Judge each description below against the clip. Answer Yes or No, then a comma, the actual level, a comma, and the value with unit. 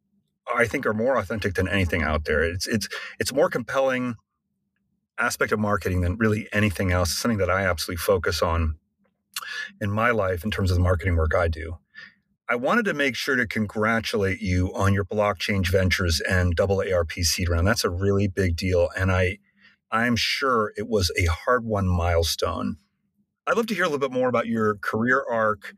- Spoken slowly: No, average, 200 wpm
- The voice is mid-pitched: No, low, 100 Hz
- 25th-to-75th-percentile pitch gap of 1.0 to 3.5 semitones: No, average, 4.0 semitones